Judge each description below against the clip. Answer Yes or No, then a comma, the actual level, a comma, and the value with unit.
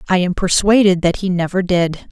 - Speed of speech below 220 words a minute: Yes, average, 200 wpm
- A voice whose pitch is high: No, medium, 180 Hz